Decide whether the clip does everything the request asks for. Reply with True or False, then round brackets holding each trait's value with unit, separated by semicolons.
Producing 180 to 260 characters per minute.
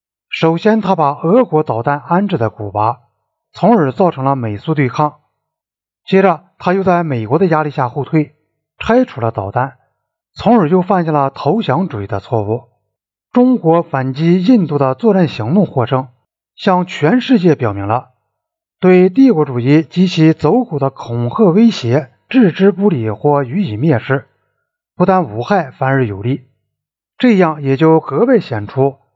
True (230 characters per minute)